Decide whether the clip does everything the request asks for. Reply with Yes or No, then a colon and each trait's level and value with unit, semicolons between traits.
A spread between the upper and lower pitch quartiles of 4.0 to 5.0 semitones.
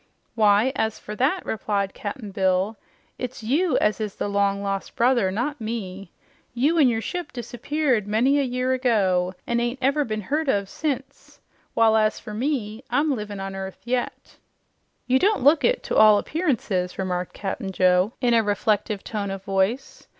Yes: average, 4.6 semitones